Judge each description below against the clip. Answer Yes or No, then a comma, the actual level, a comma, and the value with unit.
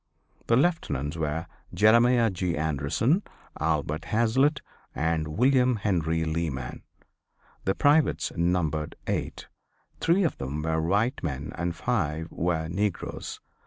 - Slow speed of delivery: Yes, slow, 115 wpm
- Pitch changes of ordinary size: No, wide, 6.8 semitones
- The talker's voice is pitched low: Yes, very low, 85 Hz